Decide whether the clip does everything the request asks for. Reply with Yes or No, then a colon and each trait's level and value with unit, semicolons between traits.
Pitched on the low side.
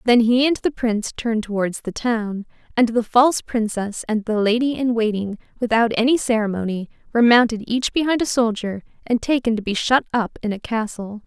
No: high, 230 Hz